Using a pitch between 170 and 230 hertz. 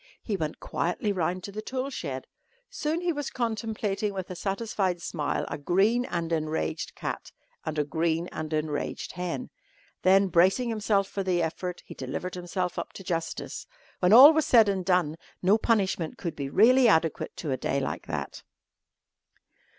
Yes: medium, 185 Hz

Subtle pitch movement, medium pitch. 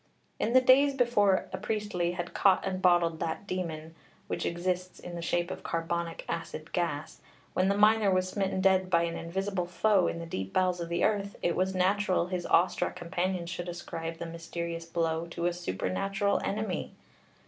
Yes: narrow, 2.3 semitones; medium, 180 Hz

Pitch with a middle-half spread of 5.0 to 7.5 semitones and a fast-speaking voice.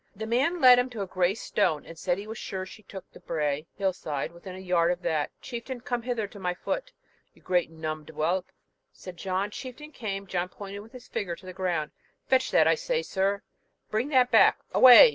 Yes: wide, 5.5 semitones; fast, 220 wpm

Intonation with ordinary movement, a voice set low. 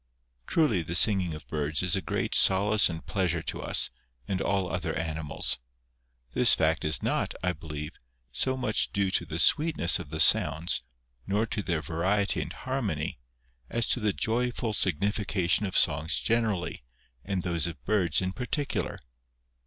Yes: average, 4.6 semitones; very low, 95 Hz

